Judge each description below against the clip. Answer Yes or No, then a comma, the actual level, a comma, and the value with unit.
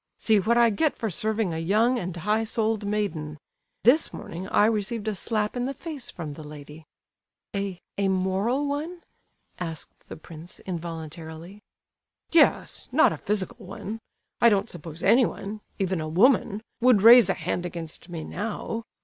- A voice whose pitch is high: Yes, high, 200 Hz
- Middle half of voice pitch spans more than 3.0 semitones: Yes, average, 4.8 semitones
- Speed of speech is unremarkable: Yes, average, 150 wpm